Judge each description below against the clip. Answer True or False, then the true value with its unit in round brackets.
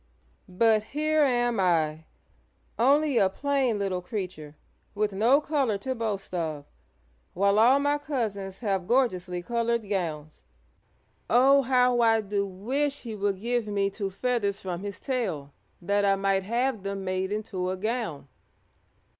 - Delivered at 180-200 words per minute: False (145 wpm)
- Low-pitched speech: False (205 Hz)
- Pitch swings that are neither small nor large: True (4.4 semitones)